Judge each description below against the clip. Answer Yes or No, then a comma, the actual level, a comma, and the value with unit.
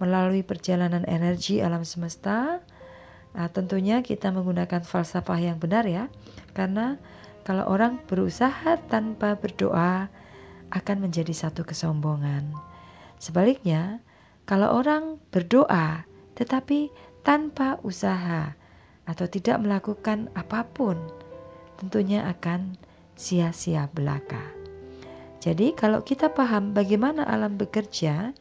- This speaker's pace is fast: No, average, 95 wpm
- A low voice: No, high, 190 Hz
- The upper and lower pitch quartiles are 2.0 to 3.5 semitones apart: No, average, 4.2 semitones